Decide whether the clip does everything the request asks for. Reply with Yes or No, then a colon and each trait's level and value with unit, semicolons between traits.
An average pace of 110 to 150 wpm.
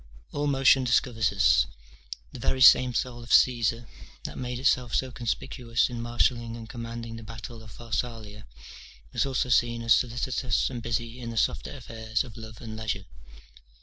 No: average, 165 wpm